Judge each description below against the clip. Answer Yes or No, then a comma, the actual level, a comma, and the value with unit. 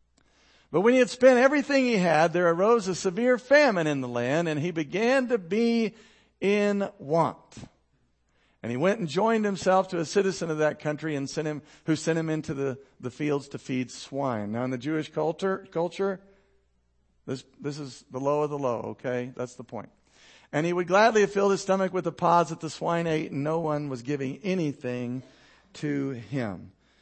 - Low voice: No, medium, 160 Hz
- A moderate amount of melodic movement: No, wide, 6.1 semitones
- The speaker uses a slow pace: No, average, 200 wpm